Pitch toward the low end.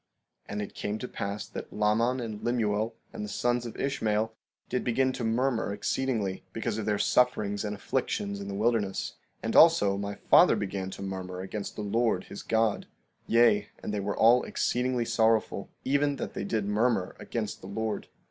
Yes: low, 110 Hz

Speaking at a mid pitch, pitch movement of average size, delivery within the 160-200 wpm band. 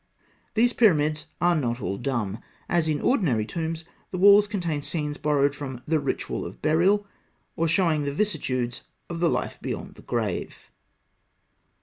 No: medium, 155 Hz; average, 3.9 semitones; average, 150 wpm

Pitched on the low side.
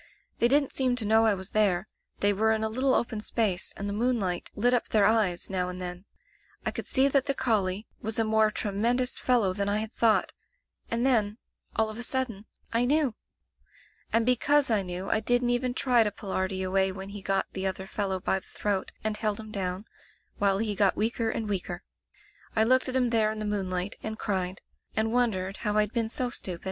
No: high, 215 Hz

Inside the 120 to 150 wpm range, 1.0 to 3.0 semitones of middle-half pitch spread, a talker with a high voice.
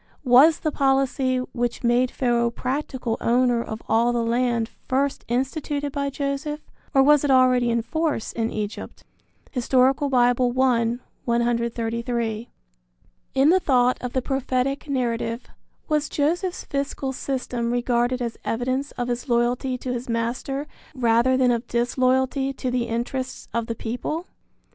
Yes: average, 140 wpm; narrow, 2.4 semitones; very high, 250 Hz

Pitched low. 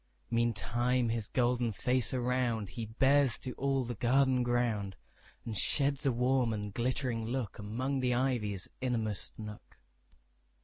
Yes: low, 120 Hz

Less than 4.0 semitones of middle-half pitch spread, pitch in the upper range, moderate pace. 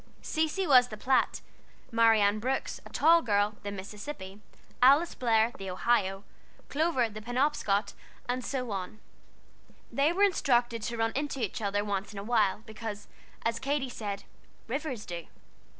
No: average, 4.6 semitones; high, 230 Hz; average, 150 wpm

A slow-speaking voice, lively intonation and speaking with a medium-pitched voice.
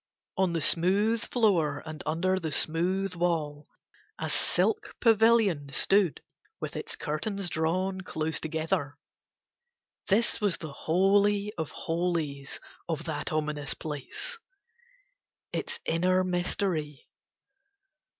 No: slow, 105 wpm; average, 4.0 semitones; medium, 175 Hz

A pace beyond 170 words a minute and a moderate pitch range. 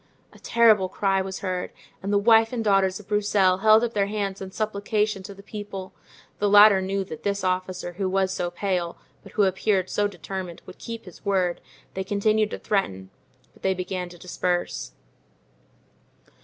No: average, 180 wpm; narrow, 2.0 semitones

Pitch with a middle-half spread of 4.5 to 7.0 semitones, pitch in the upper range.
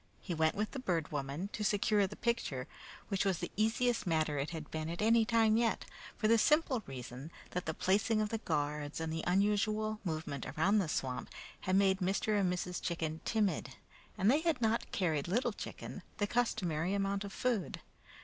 Yes: average, 5.2 semitones; high, 195 Hz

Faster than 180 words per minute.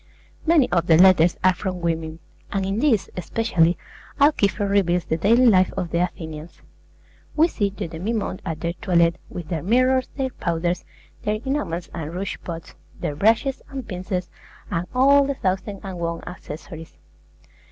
No: average, 160 wpm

